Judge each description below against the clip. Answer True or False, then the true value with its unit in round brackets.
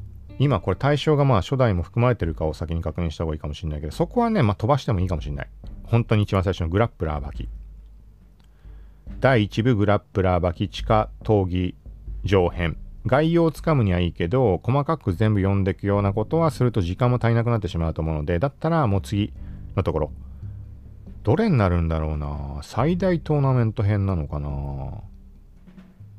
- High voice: False (100 Hz)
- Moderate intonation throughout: False (6.0 semitones)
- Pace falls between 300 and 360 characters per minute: False (390 characters per minute)